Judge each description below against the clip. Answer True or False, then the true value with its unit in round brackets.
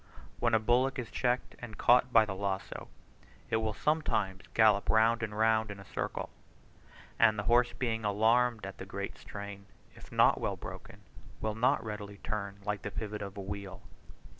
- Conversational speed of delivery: True (180 wpm)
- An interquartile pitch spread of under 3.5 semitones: True (2.5 semitones)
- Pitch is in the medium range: False (110 Hz)